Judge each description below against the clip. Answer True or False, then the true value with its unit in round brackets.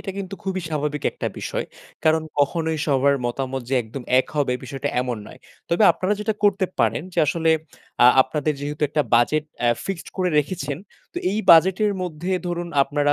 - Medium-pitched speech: True (150 Hz)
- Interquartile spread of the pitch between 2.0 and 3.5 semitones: False (4.5 semitones)